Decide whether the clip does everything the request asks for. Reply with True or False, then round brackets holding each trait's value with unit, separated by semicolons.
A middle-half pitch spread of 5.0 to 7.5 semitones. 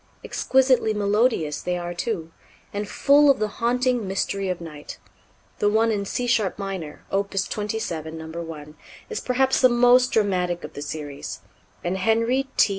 True (5.6 semitones)